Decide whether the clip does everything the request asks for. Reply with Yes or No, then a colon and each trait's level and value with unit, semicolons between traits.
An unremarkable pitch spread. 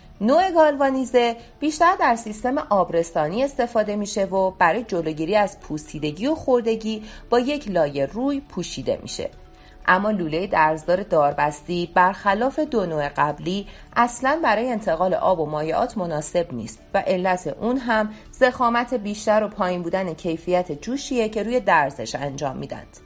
No: wide, 6.4 semitones